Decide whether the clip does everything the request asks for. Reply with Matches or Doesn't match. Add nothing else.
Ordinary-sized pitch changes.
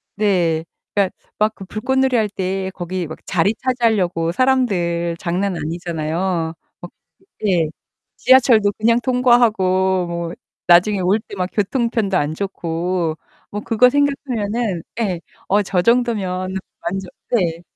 Matches